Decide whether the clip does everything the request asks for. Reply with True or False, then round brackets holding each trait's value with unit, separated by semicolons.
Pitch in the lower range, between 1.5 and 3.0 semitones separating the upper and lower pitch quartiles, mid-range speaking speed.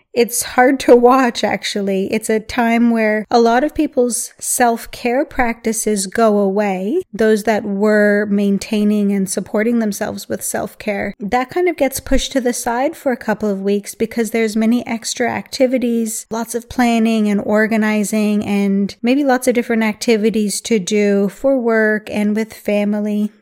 False (225 Hz; 2.6 semitones; 160 wpm)